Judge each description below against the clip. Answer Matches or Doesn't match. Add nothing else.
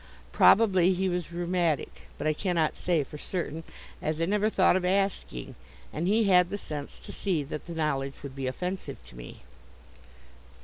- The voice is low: Doesn't match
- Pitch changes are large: Doesn't match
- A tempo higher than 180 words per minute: Doesn't match